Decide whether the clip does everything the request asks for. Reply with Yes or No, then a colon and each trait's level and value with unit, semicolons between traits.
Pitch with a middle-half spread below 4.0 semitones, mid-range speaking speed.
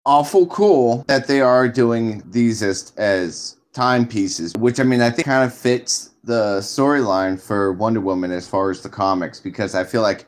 No: average, 4.7 semitones; average, 185 wpm